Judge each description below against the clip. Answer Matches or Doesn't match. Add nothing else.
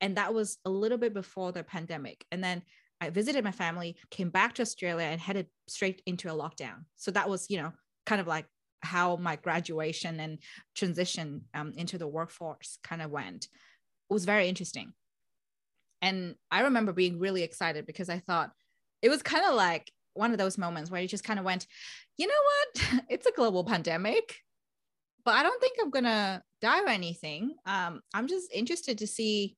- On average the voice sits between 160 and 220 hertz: Matches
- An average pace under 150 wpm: Doesn't match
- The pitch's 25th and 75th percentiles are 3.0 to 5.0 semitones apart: Matches